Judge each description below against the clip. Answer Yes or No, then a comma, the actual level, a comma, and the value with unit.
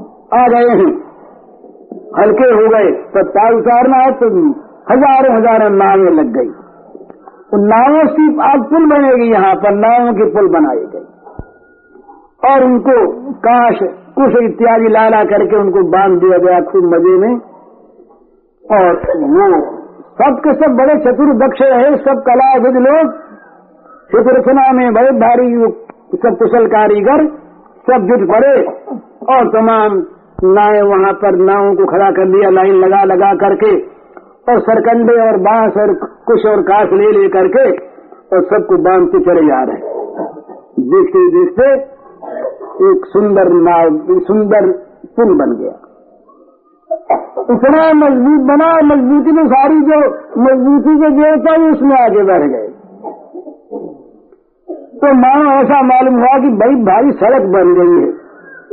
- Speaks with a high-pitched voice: Yes, very high, 265 Hz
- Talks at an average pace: Yes, average, 125 wpm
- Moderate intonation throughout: No, wide, 6.8 semitones